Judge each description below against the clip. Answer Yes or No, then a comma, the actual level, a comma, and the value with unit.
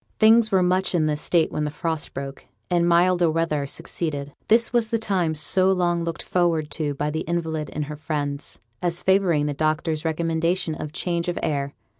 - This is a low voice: No, medium, 165 Hz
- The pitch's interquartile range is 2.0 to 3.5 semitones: Yes, average, 2.8 semitones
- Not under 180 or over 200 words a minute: Yes, average, 190 wpm